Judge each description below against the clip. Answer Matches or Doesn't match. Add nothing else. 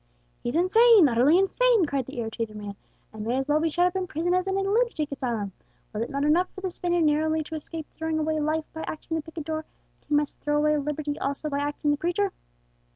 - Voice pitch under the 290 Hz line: Doesn't match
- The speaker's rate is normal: Doesn't match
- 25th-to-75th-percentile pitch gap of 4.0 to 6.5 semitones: Doesn't match